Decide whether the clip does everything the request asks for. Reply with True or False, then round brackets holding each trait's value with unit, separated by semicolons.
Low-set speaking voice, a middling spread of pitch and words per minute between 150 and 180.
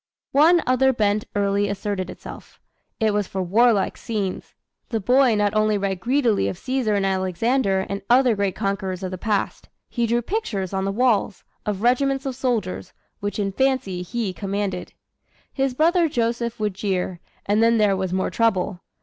False (210 Hz; 3.9 semitones; 170 wpm)